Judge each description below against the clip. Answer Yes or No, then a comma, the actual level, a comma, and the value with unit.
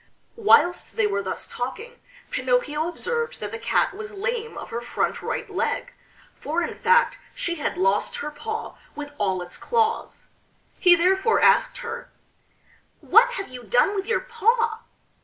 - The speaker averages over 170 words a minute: No, average, 160 wpm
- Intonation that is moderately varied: No, wide, 8.0 semitones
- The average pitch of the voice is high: Yes, very high, 395 Hz